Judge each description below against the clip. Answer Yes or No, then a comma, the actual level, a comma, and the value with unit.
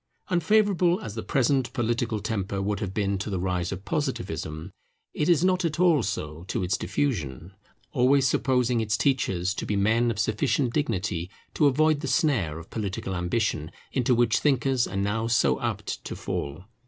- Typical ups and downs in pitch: No, wide, 6.3 semitones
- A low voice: Yes, low, 110 Hz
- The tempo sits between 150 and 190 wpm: Yes, average, 175 wpm